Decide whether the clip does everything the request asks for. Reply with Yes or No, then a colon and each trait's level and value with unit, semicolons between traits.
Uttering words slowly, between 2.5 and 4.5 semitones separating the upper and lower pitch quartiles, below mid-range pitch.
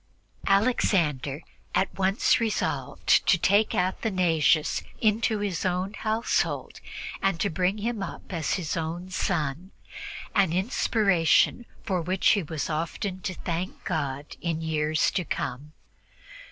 No: slow, 125 wpm; average, 3.8 semitones; medium, 185 Hz